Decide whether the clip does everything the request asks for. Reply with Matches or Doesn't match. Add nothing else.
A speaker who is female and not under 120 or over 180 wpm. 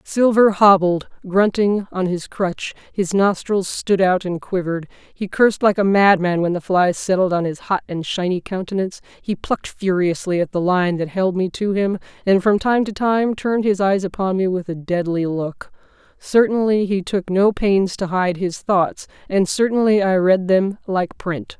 Doesn't match